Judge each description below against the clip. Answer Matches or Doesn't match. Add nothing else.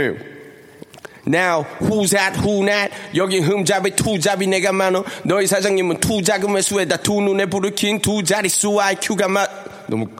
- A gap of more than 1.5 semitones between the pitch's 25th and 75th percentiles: Doesn't match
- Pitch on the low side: Doesn't match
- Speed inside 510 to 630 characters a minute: Matches